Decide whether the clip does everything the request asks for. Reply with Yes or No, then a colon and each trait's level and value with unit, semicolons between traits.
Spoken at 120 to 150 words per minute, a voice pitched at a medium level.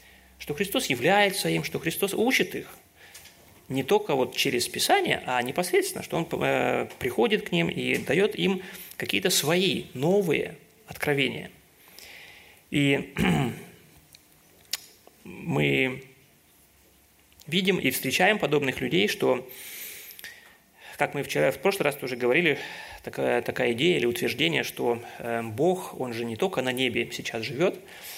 Yes: average, 125 wpm; medium, 145 Hz